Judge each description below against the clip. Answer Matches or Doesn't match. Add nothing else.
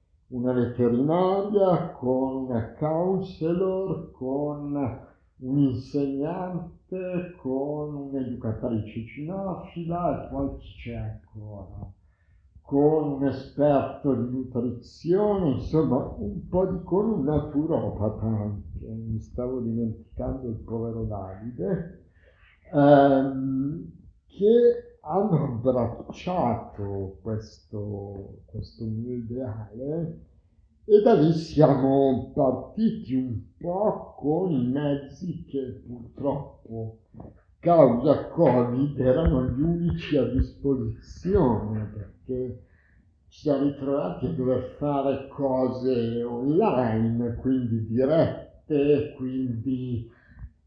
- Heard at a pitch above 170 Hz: Doesn't match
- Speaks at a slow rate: Matches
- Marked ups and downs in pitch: Doesn't match